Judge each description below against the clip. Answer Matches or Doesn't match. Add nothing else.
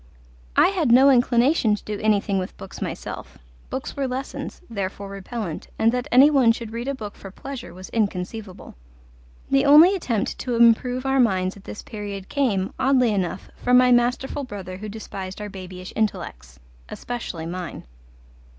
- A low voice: Doesn't match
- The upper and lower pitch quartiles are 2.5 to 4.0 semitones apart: Doesn't match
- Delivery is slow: Doesn't match